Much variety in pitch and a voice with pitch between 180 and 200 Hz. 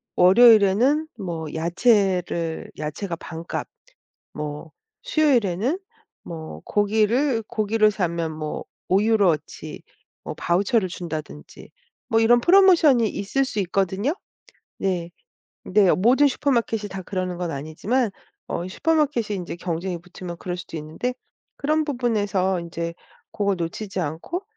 Yes: wide, 5.7 semitones; high, 195 Hz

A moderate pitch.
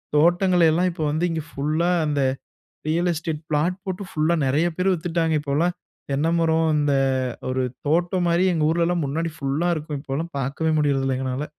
Yes: medium, 160 Hz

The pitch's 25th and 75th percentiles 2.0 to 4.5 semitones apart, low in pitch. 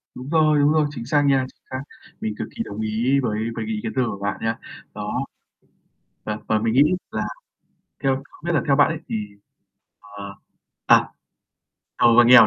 No: average, 4.9 semitones; low, 130 Hz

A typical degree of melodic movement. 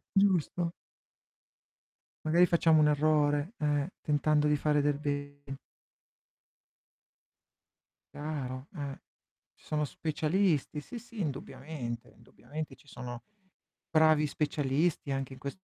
No: narrow, 1.9 semitones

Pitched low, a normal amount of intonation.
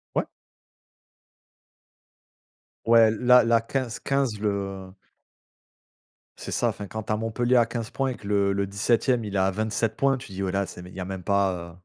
Yes: low, 110 Hz; average, 3.1 semitones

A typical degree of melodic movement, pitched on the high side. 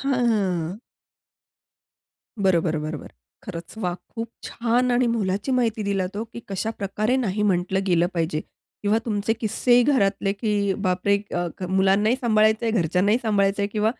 Yes: average, 3.3 semitones; high, 205 Hz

